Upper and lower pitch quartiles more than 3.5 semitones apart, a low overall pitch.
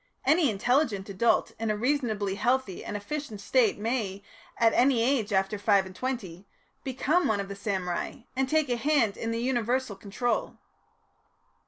No: average, 4.6 semitones; high, 230 Hz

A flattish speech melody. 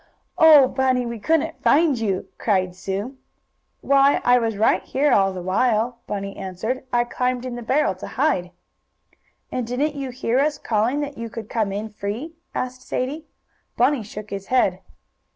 No: average, 4.4 semitones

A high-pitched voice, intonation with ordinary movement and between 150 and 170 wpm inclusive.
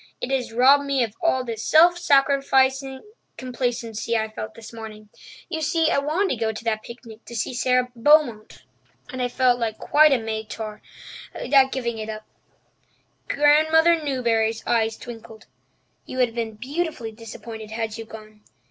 Yes: high, 240 Hz; average, 3.8 semitones; average, 165 wpm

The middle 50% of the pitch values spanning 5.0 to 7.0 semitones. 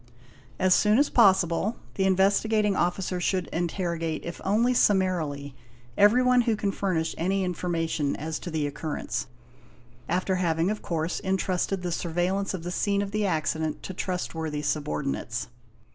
No: average, 3.4 semitones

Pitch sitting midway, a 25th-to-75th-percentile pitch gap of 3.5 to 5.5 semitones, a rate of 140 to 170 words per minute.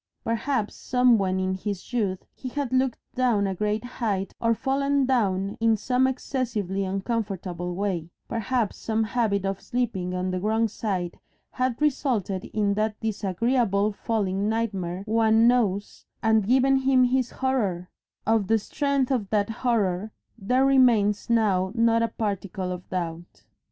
No: high, 220 Hz; average, 4.1 semitones; average, 145 wpm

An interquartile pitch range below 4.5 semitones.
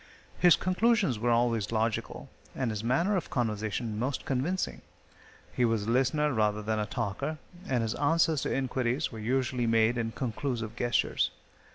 Yes: average, 3.5 semitones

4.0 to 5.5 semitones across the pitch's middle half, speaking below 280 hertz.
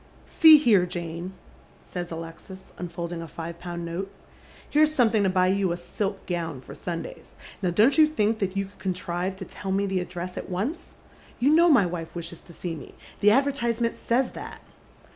Yes: average, 4.3 semitones; medium, 185 Hz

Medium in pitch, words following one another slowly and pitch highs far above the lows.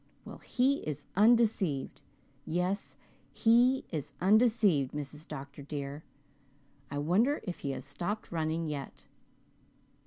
Yes: medium, 170 Hz; slow, 115 wpm; wide, 7.2 semitones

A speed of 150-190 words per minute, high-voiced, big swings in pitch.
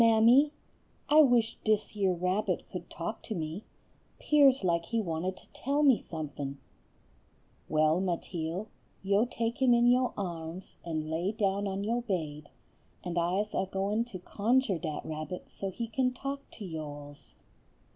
Yes: average, 155 wpm; high, 195 Hz; wide, 5.9 semitones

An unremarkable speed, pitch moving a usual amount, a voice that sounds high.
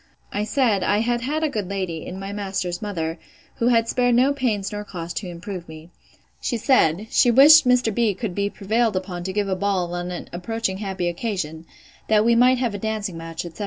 No: fast, 215 wpm; average, 4.5 semitones; high, 205 Hz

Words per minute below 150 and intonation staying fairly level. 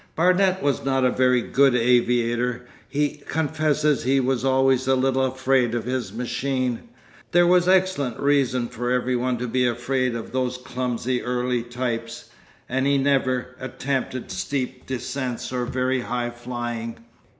Yes: average, 140 wpm; narrow, 1.6 semitones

